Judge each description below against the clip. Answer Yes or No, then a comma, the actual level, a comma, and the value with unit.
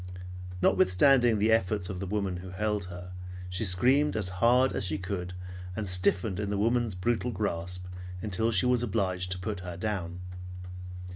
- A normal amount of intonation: Yes, average, 3.5 semitones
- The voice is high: No, low, 100 Hz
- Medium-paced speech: Yes, average, 165 wpm